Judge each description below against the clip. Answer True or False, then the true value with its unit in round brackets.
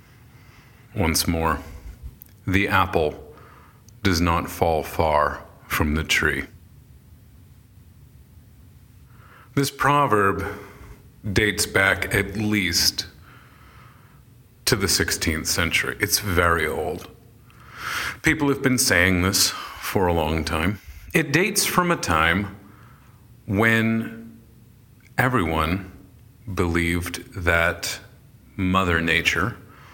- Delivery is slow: True (90 wpm)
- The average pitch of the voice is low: True (100 Hz)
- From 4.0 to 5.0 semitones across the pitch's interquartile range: False (5.5 semitones)